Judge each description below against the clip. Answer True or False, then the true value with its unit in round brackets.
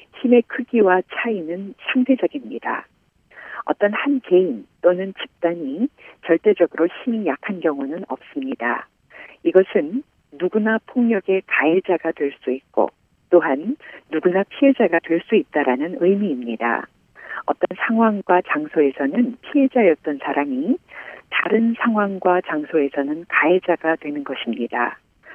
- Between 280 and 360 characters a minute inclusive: False (270 characters per minute)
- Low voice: False (190 Hz)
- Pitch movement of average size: False (7.0 semitones)